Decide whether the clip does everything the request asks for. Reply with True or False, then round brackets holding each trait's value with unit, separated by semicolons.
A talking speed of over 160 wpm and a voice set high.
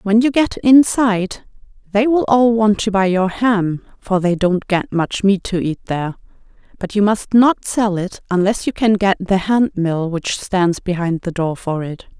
True (200 wpm; 200 Hz)